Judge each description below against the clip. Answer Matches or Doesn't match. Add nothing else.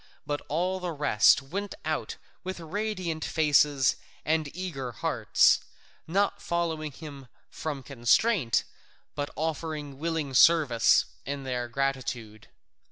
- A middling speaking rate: Doesn't match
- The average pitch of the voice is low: Doesn't match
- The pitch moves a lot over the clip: Doesn't match